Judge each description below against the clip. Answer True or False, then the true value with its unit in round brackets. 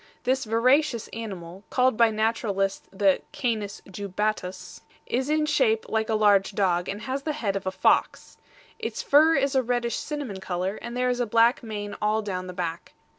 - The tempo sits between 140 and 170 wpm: False (180 wpm)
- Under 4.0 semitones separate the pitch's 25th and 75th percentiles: False (4.3 semitones)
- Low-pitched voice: False (220 Hz)